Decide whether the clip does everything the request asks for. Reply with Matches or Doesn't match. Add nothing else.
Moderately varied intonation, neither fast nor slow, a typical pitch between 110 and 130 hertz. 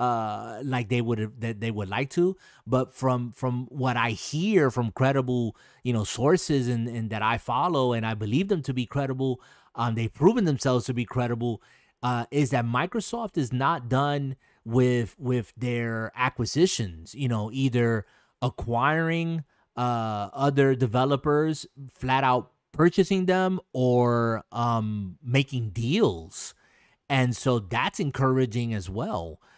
Matches